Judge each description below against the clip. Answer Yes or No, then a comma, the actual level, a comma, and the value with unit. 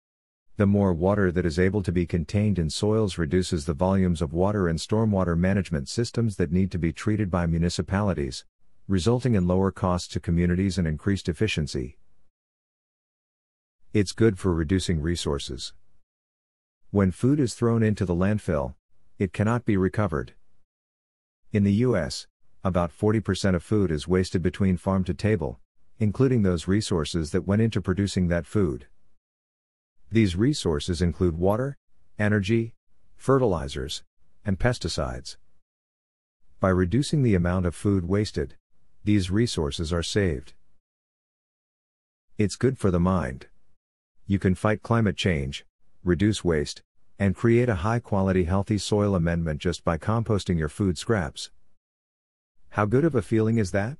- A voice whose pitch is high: No, very low, 95 Hz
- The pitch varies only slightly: No, average, 3.7 semitones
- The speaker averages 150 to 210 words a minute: No, average, 140 wpm